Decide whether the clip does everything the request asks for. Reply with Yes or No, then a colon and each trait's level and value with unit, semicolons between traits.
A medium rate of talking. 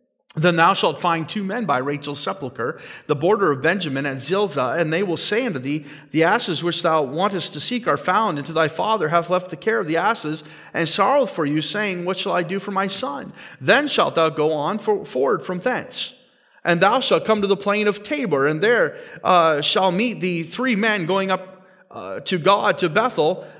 No: fast, 220 wpm